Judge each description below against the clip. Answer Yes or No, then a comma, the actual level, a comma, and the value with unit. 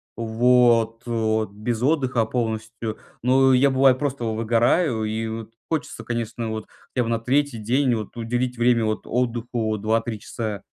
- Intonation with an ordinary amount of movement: No, narrow, 2.1 semitones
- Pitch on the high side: No, low, 115 Hz